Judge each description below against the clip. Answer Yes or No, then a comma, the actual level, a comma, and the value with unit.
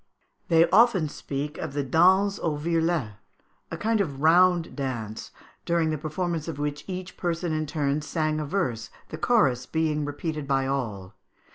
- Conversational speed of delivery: Yes, average, 160 wpm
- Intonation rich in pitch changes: No, average, 3.6 semitones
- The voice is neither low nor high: Yes, medium, 155 Hz